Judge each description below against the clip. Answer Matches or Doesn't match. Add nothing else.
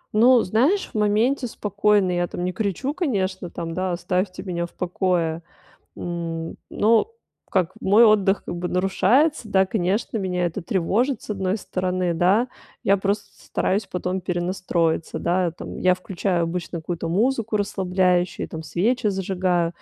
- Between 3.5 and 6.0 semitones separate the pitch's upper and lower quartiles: Doesn't match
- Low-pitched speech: Doesn't match